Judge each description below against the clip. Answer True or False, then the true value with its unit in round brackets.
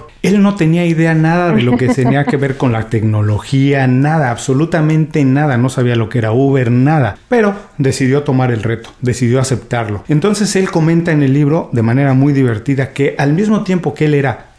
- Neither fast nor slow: False (195 wpm)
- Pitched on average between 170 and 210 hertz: False (140 Hz)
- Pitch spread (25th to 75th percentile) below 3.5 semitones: False (4.4 semitones)